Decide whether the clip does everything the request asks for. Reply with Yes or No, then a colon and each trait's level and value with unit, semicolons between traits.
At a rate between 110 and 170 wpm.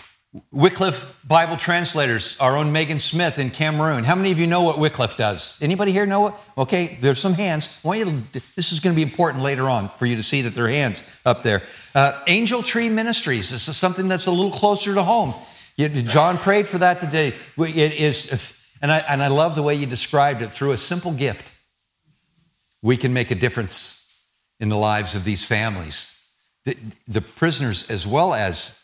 No: fast, 205 wpm